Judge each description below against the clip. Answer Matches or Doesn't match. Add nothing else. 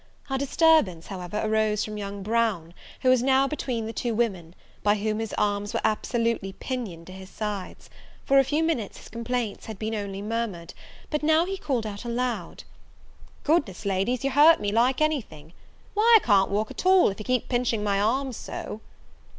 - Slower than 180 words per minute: Doesn't match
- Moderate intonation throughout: Matches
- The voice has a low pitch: Doesn't match